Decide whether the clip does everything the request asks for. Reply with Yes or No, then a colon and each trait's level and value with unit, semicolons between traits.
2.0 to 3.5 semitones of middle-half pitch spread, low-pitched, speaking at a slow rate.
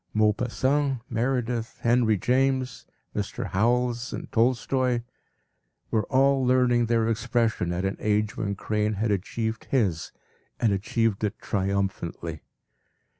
Yes: average, 3.1 semitones; low, 115 Hz; slow, 115 wpm